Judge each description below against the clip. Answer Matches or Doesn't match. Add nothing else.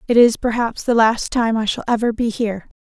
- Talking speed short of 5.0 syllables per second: Doesn't match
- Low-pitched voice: Doesn't match